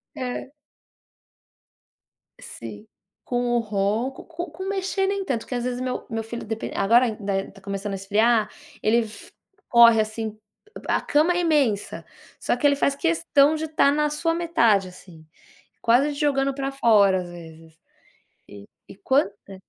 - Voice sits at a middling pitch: No, high, 235 Hz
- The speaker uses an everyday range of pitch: No, wide, 6.2 semitones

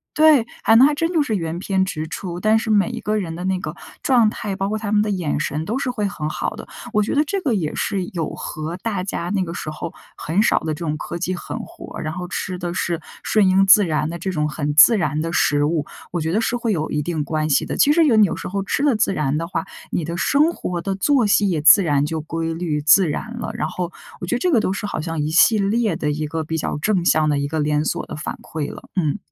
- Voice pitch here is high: No, medium, 180 Hz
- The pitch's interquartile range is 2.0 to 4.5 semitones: No, average, 5.3 semitones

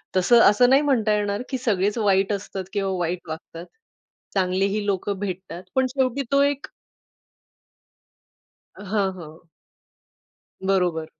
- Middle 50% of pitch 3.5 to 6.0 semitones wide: Yes, average, 4.0 semitones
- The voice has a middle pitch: No, high, 200 Hz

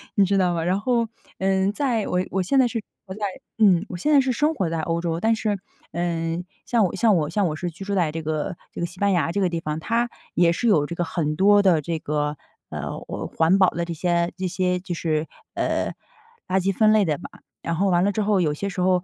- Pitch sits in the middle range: Yes, medium, 180 Hz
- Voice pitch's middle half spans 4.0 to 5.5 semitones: No, average, 3.3 semitones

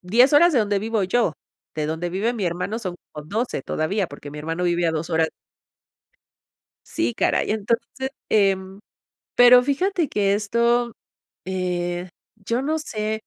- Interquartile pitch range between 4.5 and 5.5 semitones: Yes, average, 5.2 semitones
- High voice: Yes, high, 200 Hz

